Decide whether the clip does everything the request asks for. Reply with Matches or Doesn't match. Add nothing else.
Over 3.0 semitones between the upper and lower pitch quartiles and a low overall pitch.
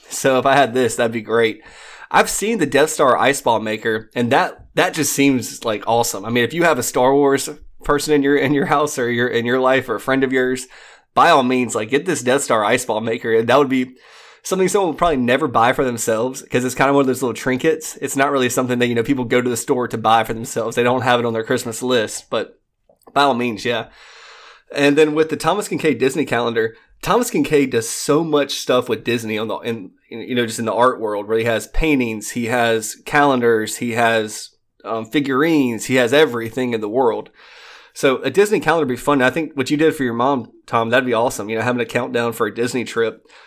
Matches